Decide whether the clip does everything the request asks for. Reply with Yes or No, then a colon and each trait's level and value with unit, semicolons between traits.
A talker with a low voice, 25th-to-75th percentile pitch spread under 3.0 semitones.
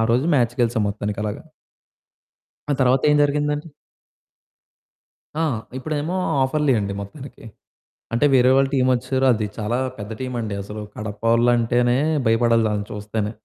No: low, 120 Hz; average, 3.7 semitones